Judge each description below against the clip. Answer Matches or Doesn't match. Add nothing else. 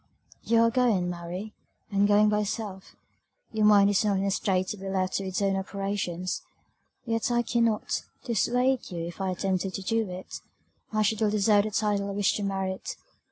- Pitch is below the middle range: Doesn't match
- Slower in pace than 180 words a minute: Doesn't match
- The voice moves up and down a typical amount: Doesn't match